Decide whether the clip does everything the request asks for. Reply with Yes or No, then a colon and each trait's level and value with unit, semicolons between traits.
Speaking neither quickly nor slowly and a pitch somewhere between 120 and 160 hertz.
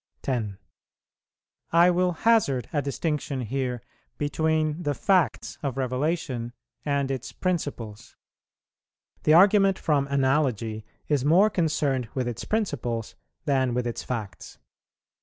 No: slow, 115 wpm; medium, 140 Hz